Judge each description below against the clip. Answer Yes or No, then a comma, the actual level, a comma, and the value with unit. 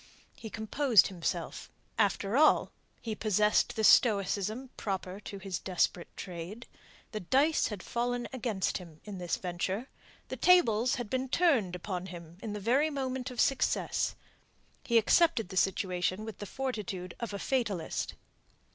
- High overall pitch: Yes, high, 210 Hz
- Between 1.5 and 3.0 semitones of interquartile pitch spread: No, average, 5.0 semitones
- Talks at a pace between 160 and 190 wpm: No, average, 145 wpm